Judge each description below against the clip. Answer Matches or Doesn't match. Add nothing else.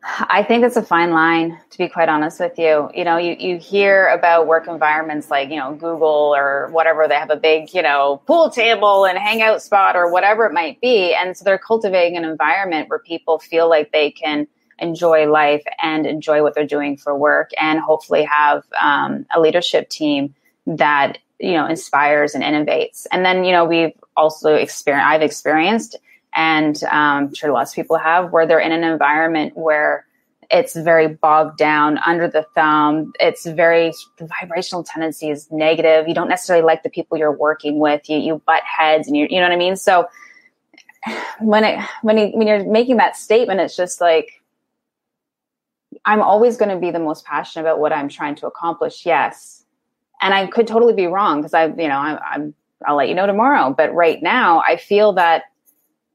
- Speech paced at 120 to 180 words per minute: Doesn't match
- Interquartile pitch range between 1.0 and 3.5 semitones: Doesn't match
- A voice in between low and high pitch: Matches